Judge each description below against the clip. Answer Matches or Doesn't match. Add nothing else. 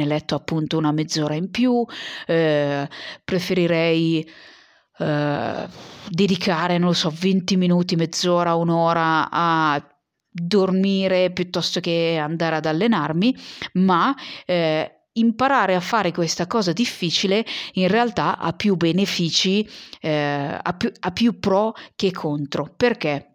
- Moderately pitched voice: Matches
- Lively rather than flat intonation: Doesn't match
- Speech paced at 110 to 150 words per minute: Matches